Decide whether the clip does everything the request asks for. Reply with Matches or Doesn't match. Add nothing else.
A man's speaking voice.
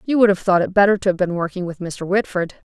Doesn't match